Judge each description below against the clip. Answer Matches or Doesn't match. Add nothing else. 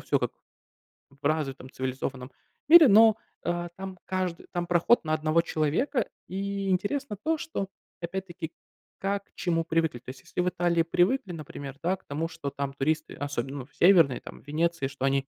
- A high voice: Doesn't match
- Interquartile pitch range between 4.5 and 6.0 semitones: Matches